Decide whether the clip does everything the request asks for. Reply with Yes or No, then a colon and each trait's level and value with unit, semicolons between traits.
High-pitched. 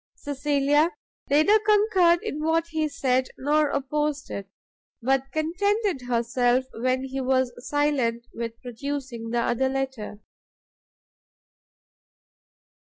Yes: very high, 270 Hz